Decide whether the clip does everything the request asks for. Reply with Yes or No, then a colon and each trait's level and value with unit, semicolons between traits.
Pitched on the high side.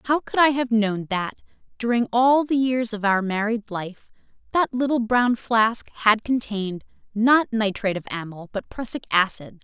Yes: high, 225 Hz